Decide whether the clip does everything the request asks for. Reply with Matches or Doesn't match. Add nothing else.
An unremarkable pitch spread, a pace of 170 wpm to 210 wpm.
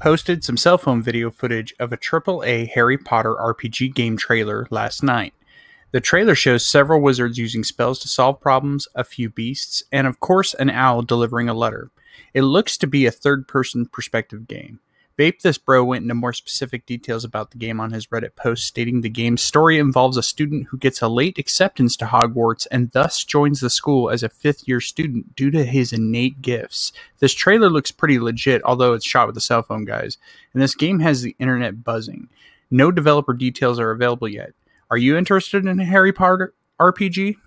Matches